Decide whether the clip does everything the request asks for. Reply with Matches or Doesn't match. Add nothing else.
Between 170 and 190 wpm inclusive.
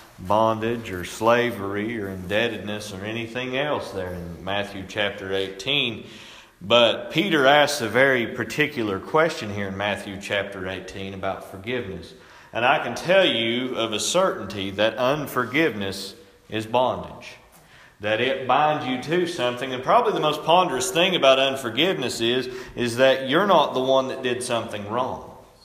Doesn't match